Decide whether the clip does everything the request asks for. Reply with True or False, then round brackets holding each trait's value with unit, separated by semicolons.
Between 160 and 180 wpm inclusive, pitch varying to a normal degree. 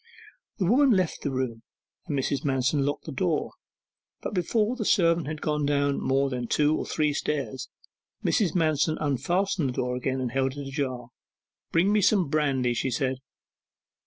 True (165 wpm; 4.0 semitones)